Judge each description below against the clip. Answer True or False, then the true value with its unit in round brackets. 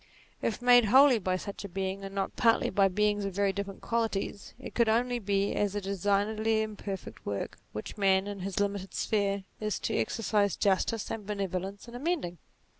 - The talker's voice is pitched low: False (200 Hz)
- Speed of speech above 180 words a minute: True (190 wpm)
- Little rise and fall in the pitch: True (2.1 semitones)